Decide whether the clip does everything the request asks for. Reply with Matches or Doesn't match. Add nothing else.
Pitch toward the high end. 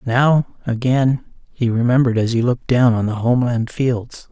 Doesn't match